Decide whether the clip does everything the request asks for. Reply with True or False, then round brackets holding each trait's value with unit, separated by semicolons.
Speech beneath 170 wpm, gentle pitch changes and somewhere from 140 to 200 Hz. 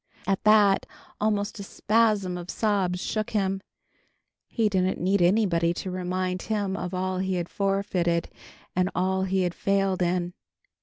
True (150 wpm; 1.8 semitones; 190 Hz)